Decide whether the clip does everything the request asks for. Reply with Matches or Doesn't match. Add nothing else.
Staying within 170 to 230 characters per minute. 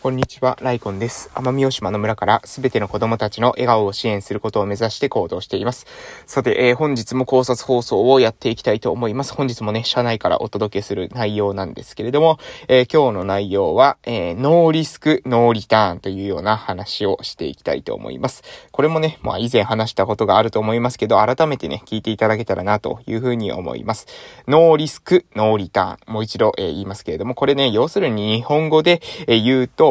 Doesn't match